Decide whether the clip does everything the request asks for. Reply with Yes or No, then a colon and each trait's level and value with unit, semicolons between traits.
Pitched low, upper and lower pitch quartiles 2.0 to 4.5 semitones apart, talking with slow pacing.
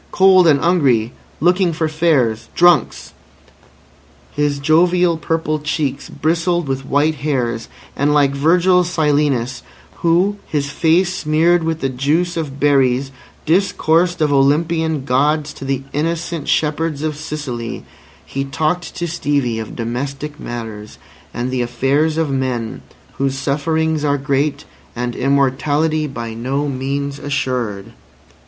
No: medium, 145 Hz; average, 3.3 semitones; slow, 125 wpm